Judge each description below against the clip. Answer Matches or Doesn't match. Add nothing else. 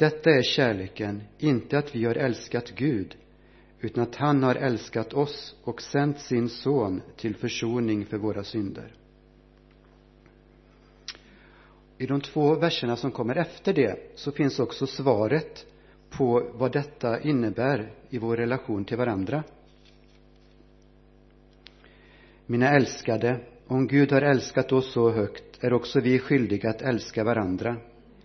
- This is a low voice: Matches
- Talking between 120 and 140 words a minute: Matches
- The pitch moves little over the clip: Doesn't match